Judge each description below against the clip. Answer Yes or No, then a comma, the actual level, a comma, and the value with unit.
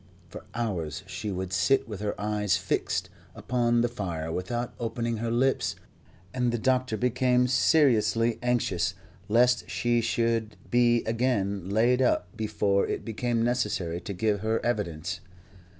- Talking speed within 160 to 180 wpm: No, average, 140 wpm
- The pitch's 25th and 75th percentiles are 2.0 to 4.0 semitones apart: Yes, average, 3.6 semitones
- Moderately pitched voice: No, low, 115 Hz